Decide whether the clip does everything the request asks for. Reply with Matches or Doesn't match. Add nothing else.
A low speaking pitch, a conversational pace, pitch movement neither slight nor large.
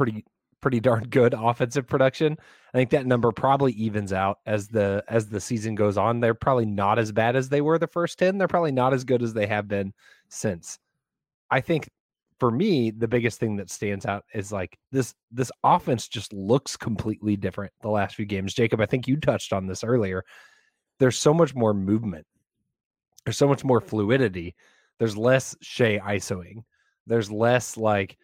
Matches